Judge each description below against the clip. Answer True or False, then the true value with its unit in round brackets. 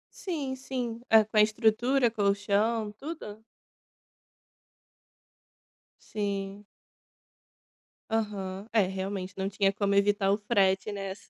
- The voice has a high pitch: True (205 Hz)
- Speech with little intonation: True (2.2 semitones)